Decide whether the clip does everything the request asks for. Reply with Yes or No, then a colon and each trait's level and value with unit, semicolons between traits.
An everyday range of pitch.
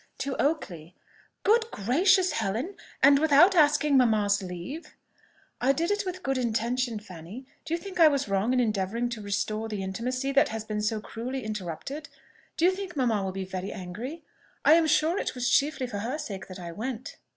No: wide, 6.6 semitones